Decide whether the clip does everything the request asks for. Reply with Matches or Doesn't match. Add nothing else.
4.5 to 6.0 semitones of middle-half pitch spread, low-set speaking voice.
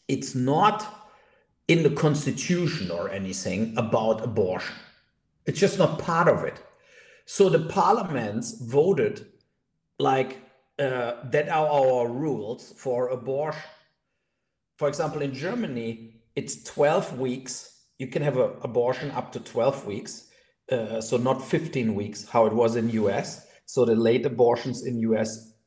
Matches